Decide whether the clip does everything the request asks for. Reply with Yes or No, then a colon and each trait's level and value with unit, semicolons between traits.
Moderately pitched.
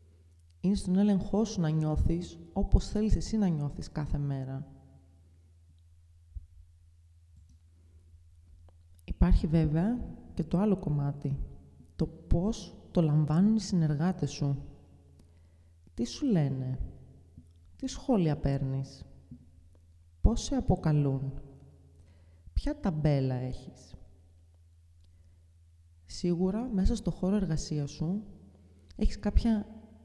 No: low, 120 Hz